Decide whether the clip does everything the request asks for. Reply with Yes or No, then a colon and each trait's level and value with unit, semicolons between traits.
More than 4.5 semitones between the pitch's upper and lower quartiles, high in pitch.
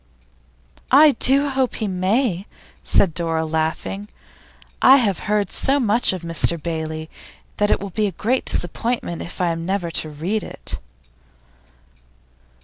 Yes: wide, 5.5 semitones; high, 195 Hz